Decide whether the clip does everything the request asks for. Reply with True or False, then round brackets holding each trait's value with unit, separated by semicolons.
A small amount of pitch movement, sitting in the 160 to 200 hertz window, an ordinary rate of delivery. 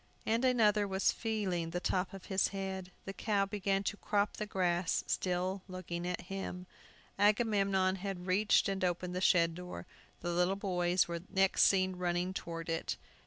True (1.9 semitones; 190 Hz; 165 wpm)